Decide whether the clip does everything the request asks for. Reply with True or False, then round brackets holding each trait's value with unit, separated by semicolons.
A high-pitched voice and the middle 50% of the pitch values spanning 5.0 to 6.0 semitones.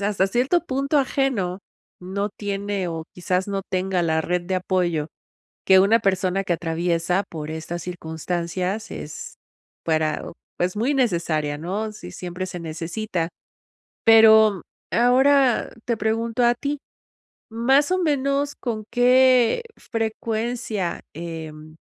True (195 Hz; 5.4 semitones)